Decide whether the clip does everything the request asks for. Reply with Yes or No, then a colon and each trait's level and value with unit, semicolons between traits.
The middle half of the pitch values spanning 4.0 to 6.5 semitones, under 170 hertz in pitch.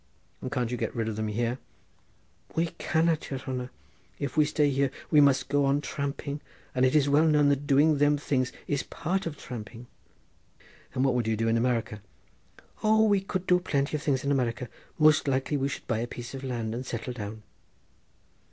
No: average, 3.3 semitones; low, 135 Hz